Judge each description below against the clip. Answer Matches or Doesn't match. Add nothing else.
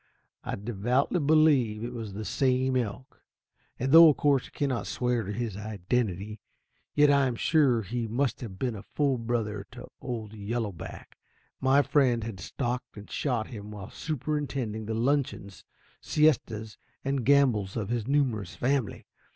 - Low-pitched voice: Matches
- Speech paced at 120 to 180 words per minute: Matches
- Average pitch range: Matches